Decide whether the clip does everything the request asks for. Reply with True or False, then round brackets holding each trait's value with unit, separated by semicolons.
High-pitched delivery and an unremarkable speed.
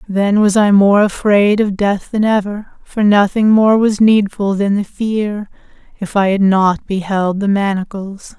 True (200 Hz; 170 wpm)